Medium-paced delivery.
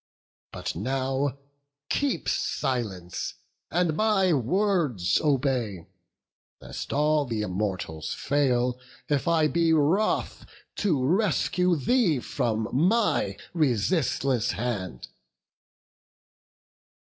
No: slow, 85 wpm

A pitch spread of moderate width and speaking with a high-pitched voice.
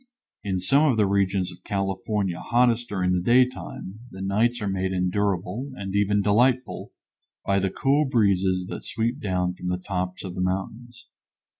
No: average, 4.0 semitones; low, 100 Hz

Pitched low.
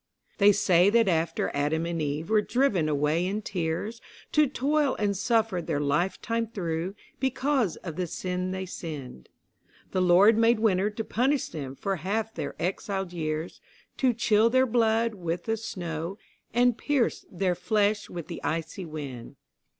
No: high, 190 Hz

